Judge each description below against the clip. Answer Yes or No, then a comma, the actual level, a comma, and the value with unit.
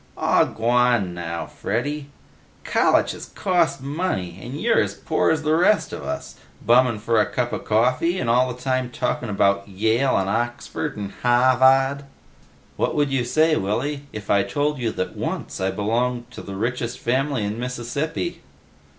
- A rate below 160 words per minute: No, average, 165 wpm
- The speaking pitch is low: Yes, low, 125 Hz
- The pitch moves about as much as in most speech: Yes, average, 4.5 semitones